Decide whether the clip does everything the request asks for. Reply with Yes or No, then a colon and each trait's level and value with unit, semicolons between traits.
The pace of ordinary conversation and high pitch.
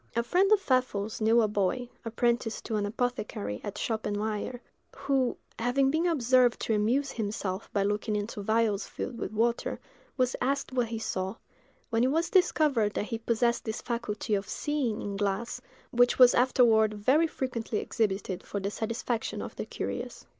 Yes: average, 170 wpm; high, 230 Hz